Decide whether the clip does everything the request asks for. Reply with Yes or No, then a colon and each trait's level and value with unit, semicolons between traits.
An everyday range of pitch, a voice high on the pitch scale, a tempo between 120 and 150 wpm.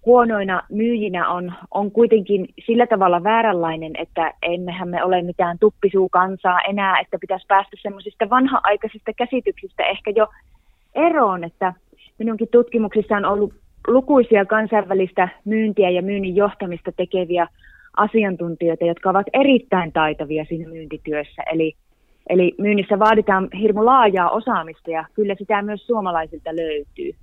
Yes: average, 3.7 semitones; high, 195 Hz; average, 125 wpm